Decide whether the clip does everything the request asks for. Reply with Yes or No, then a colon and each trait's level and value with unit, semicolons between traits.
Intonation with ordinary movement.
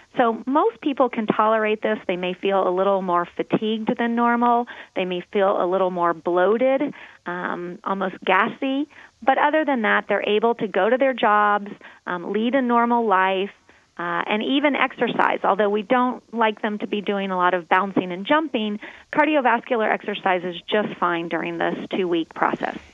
Yes: average, 4.9 semitones